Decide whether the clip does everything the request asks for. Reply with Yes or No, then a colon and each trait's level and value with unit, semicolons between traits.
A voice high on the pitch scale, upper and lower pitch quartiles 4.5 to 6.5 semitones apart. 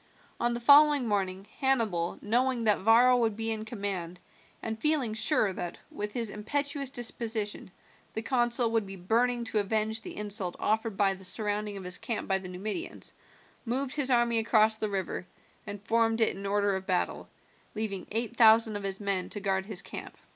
No: high, 220 Hz; average, 3.0 semitones